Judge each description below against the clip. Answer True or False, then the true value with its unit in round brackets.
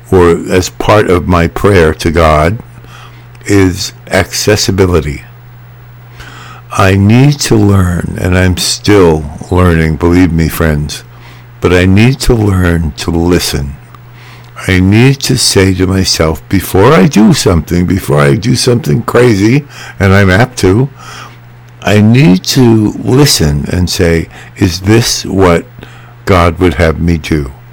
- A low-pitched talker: True (95 Hz)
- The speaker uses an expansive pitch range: True (6.0 semitones)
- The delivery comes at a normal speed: False (130 wpm)